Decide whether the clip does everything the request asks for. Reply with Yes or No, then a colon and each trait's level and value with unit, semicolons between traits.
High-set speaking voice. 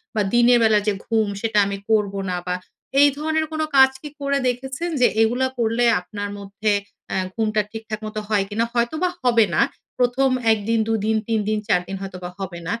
Yes: high, 225 Hz